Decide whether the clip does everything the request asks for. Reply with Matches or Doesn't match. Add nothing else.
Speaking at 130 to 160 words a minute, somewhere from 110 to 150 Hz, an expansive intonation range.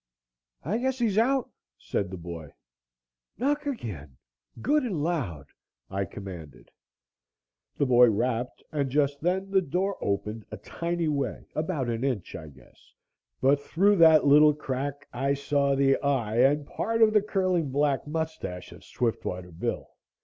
Matches